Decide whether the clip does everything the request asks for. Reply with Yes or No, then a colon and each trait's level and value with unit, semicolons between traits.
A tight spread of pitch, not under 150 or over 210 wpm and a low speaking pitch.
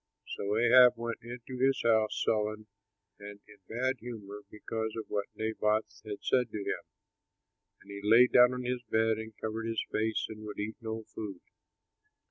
Yes: narrow, 1.9 semitones; average, 170 wpm; low, 110 Hz